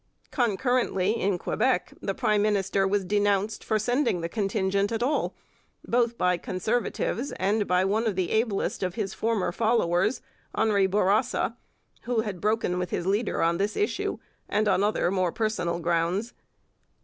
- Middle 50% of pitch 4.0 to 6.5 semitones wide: No, average, 3.2 semitones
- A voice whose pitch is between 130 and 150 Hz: No, high, 205 Hz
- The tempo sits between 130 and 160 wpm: Yes, average, 155 wpm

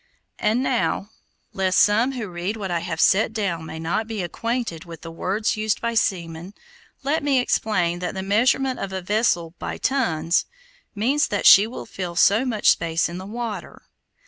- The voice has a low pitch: No, high, 205 Hz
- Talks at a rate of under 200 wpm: Yes, average, 180 wpm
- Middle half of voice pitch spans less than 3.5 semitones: No, average, 4.7 semitones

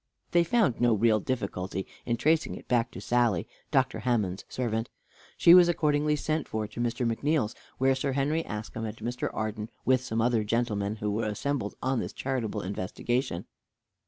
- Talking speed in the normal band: Yes, average, 165 wpm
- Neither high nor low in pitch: No, low, 120 Hz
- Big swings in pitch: No, average, 3.8 semitones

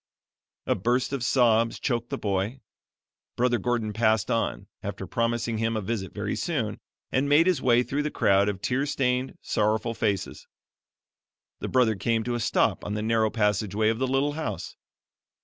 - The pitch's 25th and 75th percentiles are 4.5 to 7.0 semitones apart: No, average, 2.9 semitones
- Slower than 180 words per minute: Yes, average, 170 wpm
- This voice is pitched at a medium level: No, low, 115 Hz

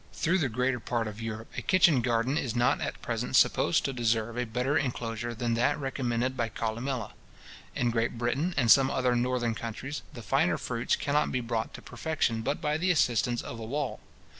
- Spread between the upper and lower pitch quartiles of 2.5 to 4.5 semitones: Yes, average, 2.8 semitones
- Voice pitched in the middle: No, low, 120 Hz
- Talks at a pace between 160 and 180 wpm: No, average, 195 wpm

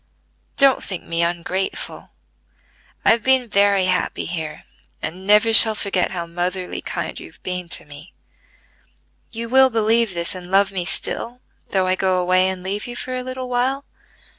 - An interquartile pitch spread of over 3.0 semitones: Yes, average, 4.3 semitones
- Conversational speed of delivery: Yes, average, 170 wpm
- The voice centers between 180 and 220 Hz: Yes, high, 190 Hz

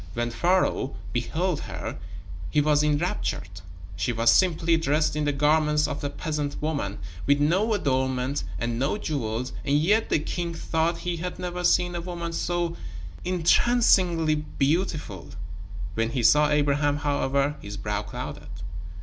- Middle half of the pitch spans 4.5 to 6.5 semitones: No, average, 3.8 semitones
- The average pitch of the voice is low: No, medium, 150 Hz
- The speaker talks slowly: No, average, 145 wpm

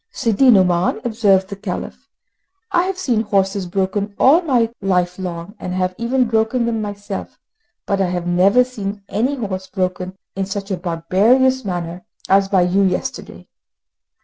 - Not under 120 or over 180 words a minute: Yes, average, 155 wpm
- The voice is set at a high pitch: Yes, high, 200 Hz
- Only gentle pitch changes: No, average, 3.8 semitones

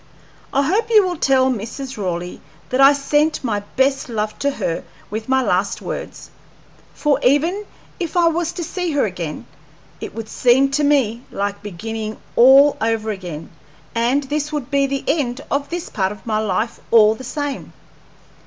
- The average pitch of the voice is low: No, very high, 260 Hz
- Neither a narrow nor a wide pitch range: Yes, average, 5.0 semitones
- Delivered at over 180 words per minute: No, average, 170 wpm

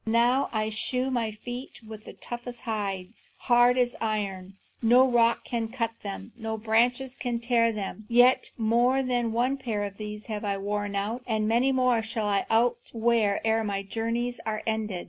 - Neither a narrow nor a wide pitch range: No, narrow, 2.3 semitones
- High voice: Yes, high, 225 Hz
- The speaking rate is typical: Yes, average, 170 wpm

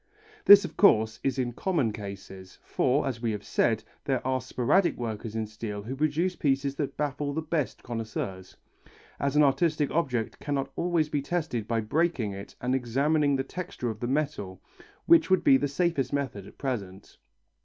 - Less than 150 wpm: No, average, 175 wpm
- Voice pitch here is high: No, low, 135 Hz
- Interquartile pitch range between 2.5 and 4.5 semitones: No, average, 5.1 semitones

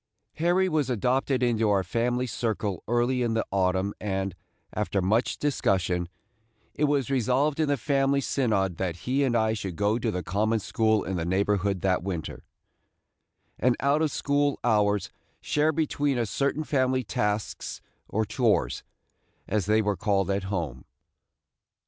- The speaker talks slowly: No, average, 155 wpm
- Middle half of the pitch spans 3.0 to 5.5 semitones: Yes, average, 5.2 semitones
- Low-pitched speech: Yes, low, 110 Hz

